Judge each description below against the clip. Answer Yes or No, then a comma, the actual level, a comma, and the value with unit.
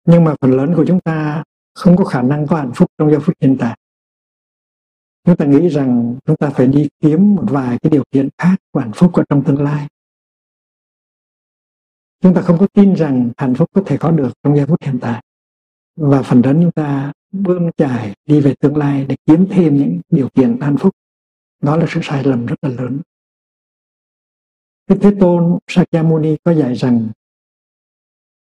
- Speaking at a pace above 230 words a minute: No, average, 195 wpm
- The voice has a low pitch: No, medium, 150 Hz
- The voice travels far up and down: No, average, 4.2 semitones